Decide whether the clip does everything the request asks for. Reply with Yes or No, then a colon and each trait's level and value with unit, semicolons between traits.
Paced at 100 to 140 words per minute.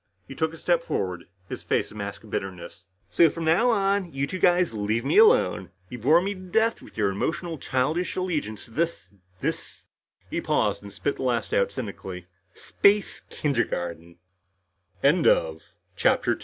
No: average, 155 wpm